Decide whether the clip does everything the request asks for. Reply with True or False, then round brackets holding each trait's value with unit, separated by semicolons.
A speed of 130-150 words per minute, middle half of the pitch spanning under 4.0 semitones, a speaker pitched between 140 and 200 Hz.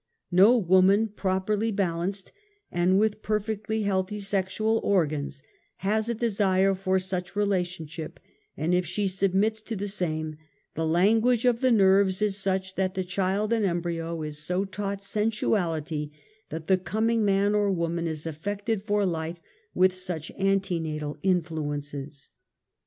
True (145 wpm; 3.4 semitones; 190 Hz)